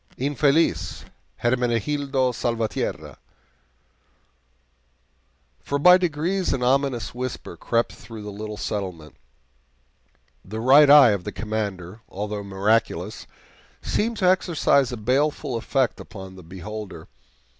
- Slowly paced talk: Yes, slow, 105 wpm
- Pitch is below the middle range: Yes, low, 120 Hz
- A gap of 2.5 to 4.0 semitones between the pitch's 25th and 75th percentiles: No, wide, 5.4 semitones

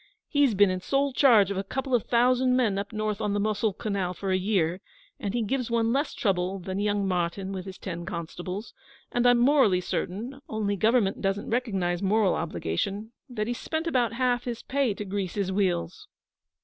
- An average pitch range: Yes, average, 4.2 semitones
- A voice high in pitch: Yes, high, 205 Hz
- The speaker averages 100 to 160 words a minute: No, average, 195 wpm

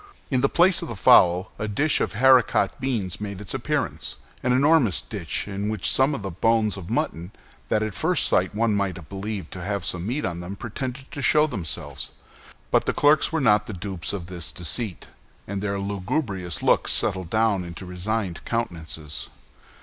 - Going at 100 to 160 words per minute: No, average, 180 wpm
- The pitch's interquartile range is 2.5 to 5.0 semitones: Yes, average, 4.7 semitones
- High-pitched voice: No, low, 100 Hz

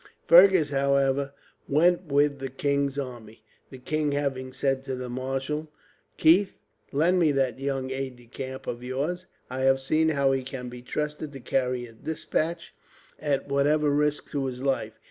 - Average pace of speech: Yes, average, 165 wpm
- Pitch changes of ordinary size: No, narrow, 2.3 semitones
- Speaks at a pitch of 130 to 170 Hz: Yes, medium, 140 Hz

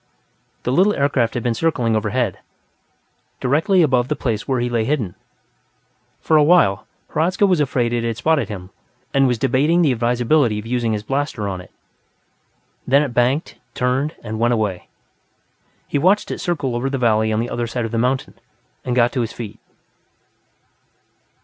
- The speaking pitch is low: Yes, low, 125 Hz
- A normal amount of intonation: Yes, average, 3.9 semitones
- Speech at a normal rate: Yes, average, 175 wpm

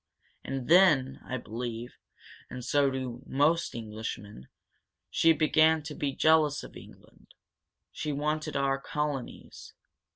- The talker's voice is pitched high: No, medium, 140 Hz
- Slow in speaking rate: Yes, slow, 120 wpm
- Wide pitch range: No, average, 3.6 semitones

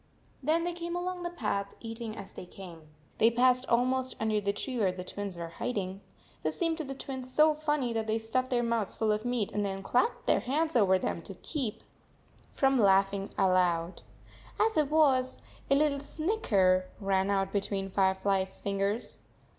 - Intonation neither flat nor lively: No, wide, 5.7 semitones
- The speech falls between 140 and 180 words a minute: No, average, 190 wpm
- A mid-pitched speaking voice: No, high, 225 Hz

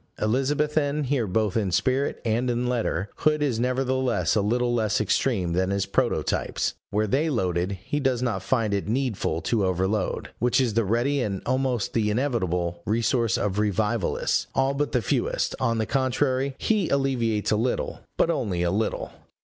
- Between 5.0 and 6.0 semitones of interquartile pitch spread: No, average, 4.4 semitones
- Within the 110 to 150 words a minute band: No, average, 170 wpm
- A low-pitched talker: Yes, low, 115 Hz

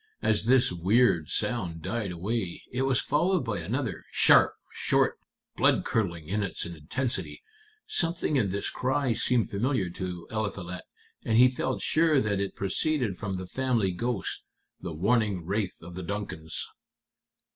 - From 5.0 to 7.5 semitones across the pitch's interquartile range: Yes, wide, 5.6 semitones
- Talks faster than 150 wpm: No, average, 145 wpm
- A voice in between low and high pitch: No, low, 105 Hz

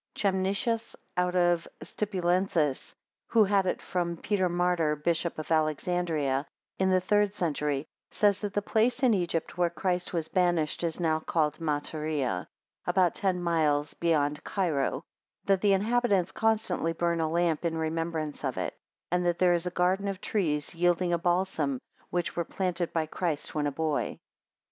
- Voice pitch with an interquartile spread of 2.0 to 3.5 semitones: Yes, average, 3.0 semitones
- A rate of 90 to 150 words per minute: No, average, 160 wpm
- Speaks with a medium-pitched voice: Yes, medium, 175 Hz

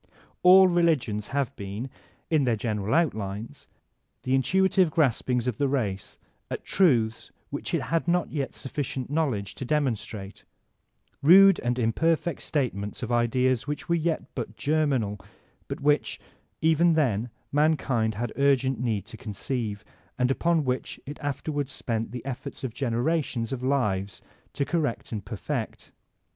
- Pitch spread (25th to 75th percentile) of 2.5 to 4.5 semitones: No, average, 5.2 semitones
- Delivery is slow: No, average, 150 wpm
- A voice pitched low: Yes, low, 130 Hz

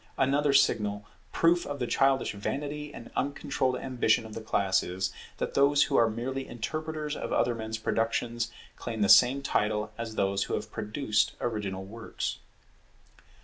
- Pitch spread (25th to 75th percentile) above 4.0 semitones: Yes, average, 4.4 semitones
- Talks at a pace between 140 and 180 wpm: Yes, average, 155 wpm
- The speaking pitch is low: Yes, low, 120 Hz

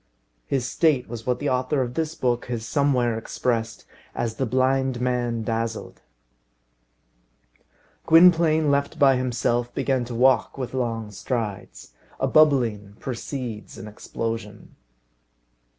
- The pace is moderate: No, slow, 120 wpm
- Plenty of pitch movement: No, average, 2.8 semitones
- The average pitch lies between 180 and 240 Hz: No, low, 125 Hz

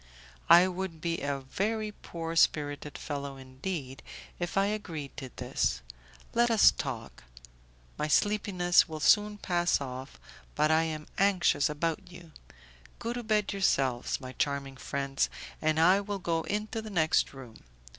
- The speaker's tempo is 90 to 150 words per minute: Yes, average, 145 wpm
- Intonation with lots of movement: Yes, wide, 5.8 semitones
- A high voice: No, medium, 165 Hz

